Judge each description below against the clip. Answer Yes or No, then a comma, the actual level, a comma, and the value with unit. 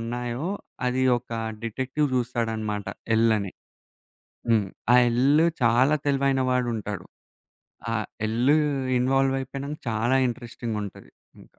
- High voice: No, low, 120 Hz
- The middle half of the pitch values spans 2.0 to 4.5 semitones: Yes, average, 2.8 semitones